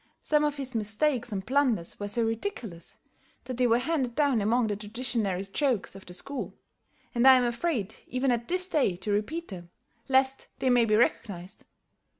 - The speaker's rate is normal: Yes, average, 180 wpm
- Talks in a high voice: Yes, high, 240 Hz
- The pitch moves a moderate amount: Yes, average, 4.6 semitones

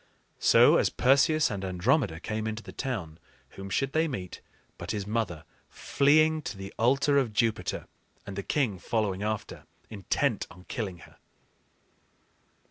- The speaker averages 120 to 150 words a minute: Yes, average, 145 wpm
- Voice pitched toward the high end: No, low, 110 Hz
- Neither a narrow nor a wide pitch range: No, wide, 5.9 semitones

